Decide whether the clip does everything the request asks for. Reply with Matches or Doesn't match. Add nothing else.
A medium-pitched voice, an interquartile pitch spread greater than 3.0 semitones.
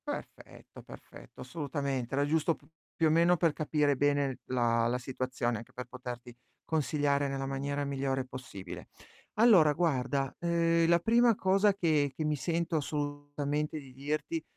Matches